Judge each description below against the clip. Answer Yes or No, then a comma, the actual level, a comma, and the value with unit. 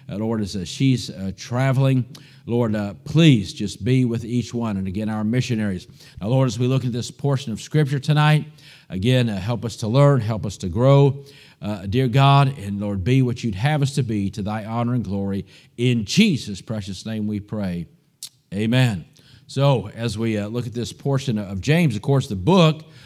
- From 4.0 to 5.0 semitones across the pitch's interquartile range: Yes, average, 4.6 semitones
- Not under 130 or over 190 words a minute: No, fast, 205 wpm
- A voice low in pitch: Yes, low, 120 Hz